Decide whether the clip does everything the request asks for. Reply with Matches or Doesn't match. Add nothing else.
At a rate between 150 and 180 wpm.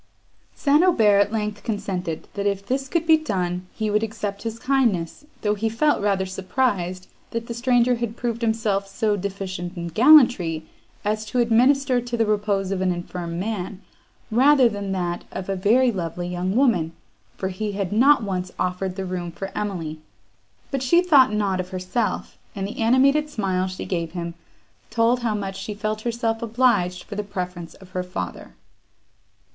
Matches